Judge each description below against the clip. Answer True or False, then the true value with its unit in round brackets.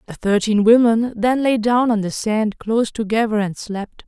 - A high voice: True (220 Hz)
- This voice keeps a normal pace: True (190 wpm)